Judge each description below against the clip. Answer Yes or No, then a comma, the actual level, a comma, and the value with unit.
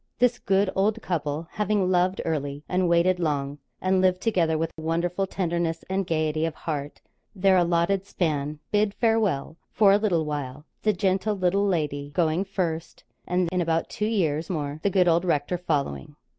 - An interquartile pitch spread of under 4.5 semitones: Yes, average, 3.6 semitones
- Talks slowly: No, average, 165 wpm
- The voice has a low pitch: No, medium, 175 Hz